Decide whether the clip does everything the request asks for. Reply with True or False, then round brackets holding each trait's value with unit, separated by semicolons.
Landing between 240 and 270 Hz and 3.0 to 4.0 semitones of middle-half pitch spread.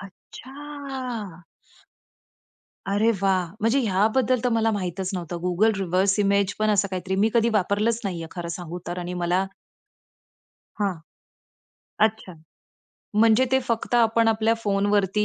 False (205 Hz; 3.3 semitones)